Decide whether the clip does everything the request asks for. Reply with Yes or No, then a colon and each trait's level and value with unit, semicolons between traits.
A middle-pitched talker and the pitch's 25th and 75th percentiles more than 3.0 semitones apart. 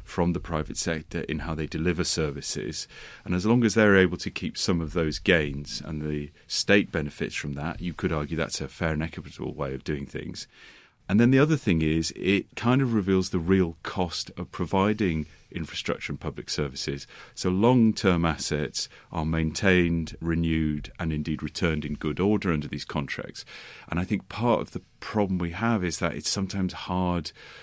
No: very low, 85 Hz; average, 3.6 semitones